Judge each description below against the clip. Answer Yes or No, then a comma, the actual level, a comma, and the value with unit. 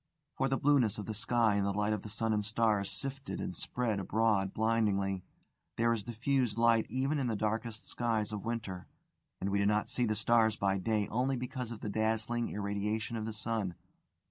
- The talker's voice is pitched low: Yes, low, 110 Hz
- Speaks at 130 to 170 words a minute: No, average, 200 wpm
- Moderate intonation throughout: No, narrow, 2.3 semitones